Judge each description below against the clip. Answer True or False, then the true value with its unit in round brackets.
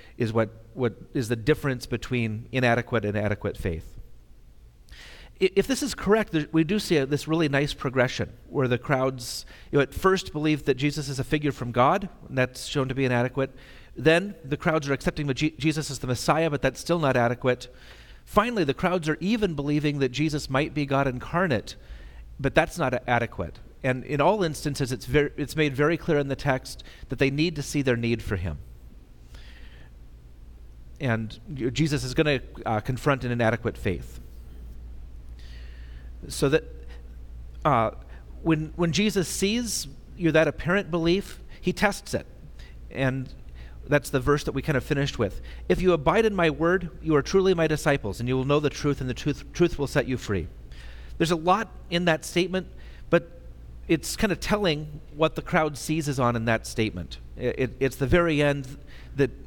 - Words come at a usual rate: True (185 wpm)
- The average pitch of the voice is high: False (135 Hz)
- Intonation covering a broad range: True (5.9 semitones)